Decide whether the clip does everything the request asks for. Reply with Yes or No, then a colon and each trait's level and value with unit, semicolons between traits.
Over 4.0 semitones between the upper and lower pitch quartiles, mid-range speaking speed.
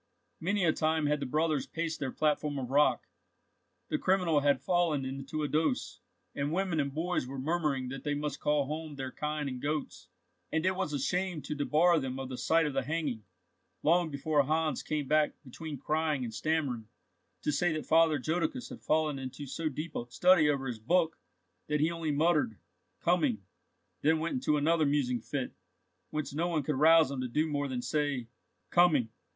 No: average, 2.9 semitones; average, 190 wpm